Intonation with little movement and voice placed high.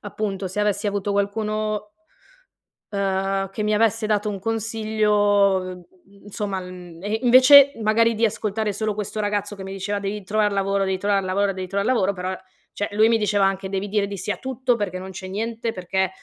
Yes: narrow, 1.9 semitones; high, 205 Hz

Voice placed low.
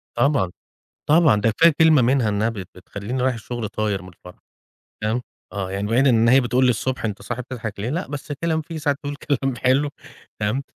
Yes: low, 120 Hz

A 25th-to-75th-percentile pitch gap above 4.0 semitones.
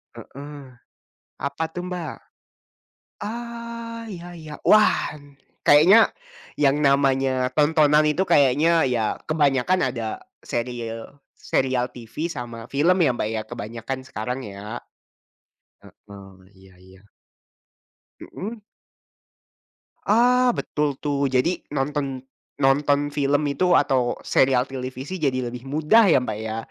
Yes: average, 4.6 semitones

